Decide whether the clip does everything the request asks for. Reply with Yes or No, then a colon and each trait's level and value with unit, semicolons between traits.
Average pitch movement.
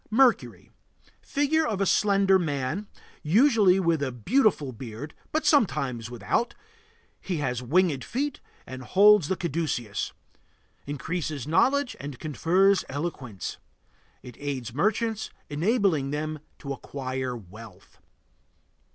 No: wide, 7.4 semitones